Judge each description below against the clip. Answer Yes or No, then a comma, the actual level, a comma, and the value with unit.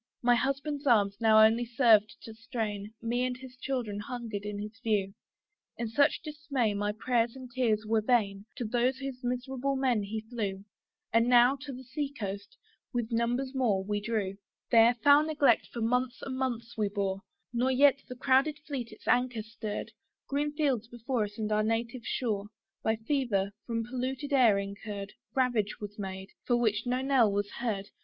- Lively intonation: No, average, 3.5 semitones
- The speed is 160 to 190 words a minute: Yes, average, 180 wpm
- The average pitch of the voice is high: Yes, high, 235 Hz